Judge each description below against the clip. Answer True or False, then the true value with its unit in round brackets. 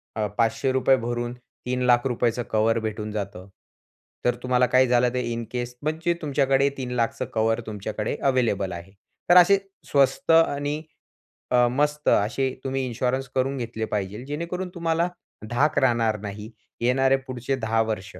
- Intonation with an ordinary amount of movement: True (3.3 semitones)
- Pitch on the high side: False (125 Hz)